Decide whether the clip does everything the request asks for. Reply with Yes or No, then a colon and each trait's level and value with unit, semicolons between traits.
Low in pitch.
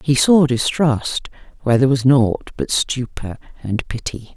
Yes: low, 130 Hz